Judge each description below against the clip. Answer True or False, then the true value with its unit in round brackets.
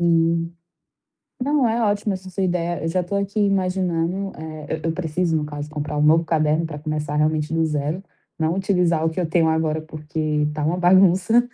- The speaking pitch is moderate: True (165 Hz)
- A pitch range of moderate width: True (3.2 semitones)